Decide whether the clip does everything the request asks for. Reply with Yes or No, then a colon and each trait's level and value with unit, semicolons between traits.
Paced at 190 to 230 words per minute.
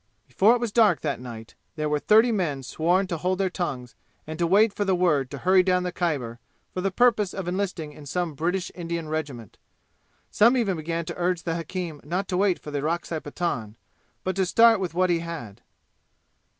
Yes: fast, 205 wpm